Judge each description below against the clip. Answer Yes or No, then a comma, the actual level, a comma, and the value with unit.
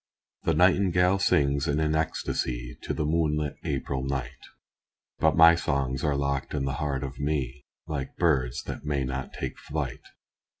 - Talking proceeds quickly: No, average, 160 wpm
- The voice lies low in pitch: Yes, very low, 70 Hz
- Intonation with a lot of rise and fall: No, narrow, 2.6 semitones